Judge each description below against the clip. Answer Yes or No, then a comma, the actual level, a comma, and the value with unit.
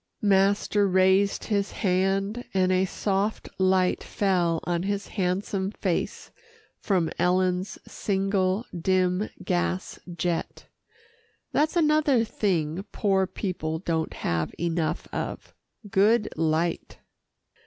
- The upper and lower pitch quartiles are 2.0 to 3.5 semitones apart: Yes, narrow, 2.4 semitones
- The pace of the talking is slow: Yes, slow, 100 wpm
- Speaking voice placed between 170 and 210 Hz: Yes, high, 190 Hz